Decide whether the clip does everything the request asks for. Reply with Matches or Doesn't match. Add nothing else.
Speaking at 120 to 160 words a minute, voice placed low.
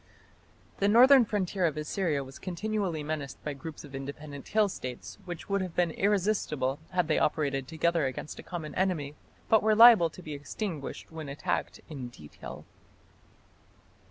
Doesn't match